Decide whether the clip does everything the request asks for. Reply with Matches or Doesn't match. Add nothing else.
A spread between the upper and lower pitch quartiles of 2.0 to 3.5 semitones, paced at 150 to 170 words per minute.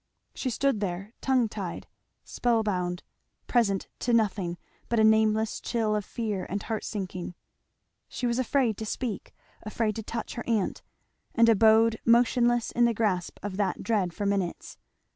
Matches